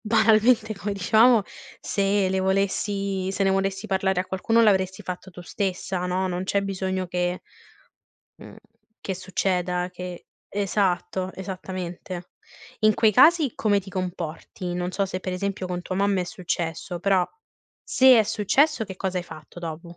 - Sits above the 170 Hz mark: Yes, high, 190 Hz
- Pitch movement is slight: Yes, narrow, 1.8 semitones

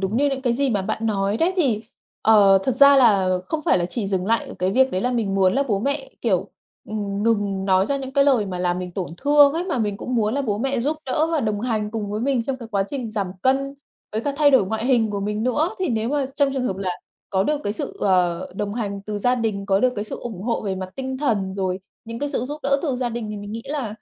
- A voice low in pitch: No, high, 225 Hz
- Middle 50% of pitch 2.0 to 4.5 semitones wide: No, average, 5.2 semitones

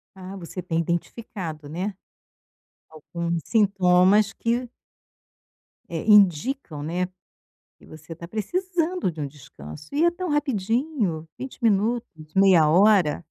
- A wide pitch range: Yes, wide, 5.9 semitones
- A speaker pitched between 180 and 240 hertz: Yes, high, 190 Hz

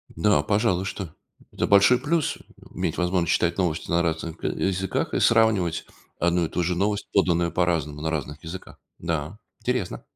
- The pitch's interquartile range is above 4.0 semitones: No, average, 3.4 semitones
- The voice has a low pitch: Yes, very low, 90 Hz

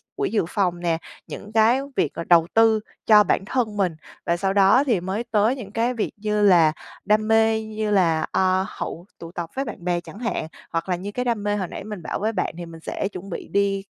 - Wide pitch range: No, average, 3.8 semitones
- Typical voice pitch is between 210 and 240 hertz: No, high, 200 Hz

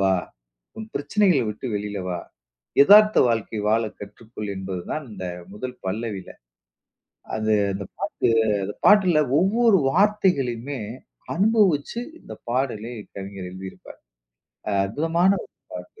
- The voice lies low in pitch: Yes, low, 120 Hz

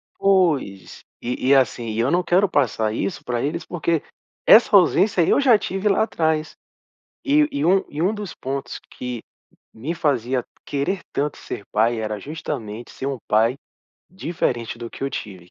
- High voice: No, medium, 145 Hz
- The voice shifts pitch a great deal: Yes, wide, 7.5 semitones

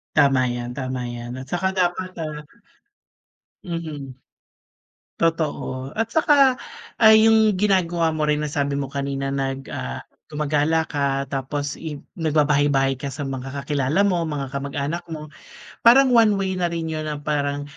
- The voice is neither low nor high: Yes, medium, 150 Hz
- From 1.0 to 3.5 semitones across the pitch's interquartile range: No, average, 3.9 semitones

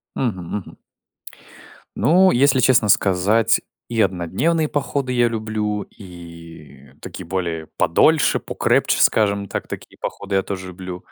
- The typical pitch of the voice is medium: No, low, 100 Hz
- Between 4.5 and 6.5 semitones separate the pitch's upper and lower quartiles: Yes, average, 5.2 semitones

